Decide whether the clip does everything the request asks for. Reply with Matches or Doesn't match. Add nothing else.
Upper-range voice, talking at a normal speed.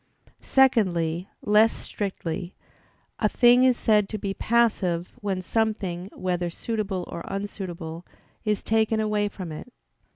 Doesn't match